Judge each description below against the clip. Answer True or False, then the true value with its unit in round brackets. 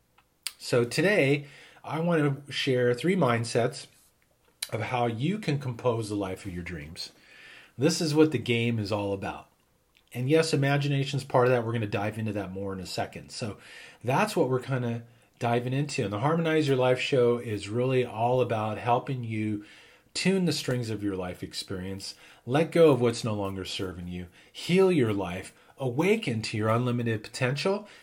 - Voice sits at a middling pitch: False (120 Hz)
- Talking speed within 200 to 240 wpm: False (185 wpm)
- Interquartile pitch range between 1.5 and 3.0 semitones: False (5.0 semitones)